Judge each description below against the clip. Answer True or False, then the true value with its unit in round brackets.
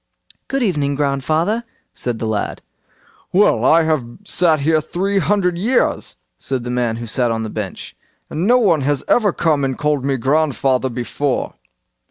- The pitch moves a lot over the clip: True (6.2 semitones)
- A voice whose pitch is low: False (145 Hz)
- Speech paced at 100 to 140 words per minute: False (160 wpm)